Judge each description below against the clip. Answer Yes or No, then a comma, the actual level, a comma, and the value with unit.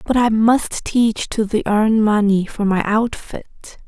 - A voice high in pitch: Yes, high, 215 Hz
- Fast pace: No, average, 170 wpm